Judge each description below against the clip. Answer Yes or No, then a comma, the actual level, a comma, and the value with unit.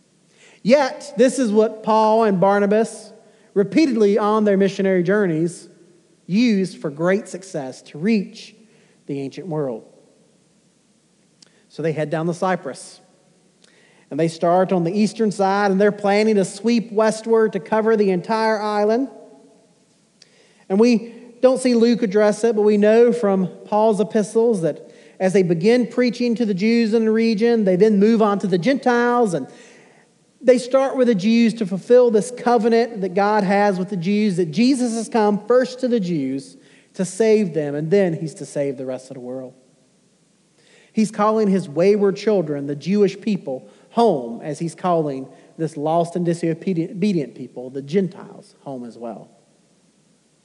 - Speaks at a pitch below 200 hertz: No, high, 205 Hz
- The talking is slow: No, average, 160 wpm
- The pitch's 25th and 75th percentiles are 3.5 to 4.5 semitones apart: Yes, average, 4.2 semitones